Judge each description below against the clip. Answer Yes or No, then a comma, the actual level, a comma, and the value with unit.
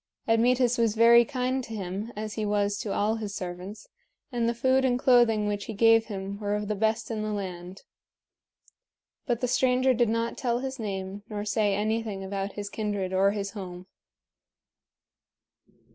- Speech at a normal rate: Yes, average, 175 wpm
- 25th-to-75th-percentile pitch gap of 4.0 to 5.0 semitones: No, average, 2.7 semitones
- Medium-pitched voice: No, high, 215 Hz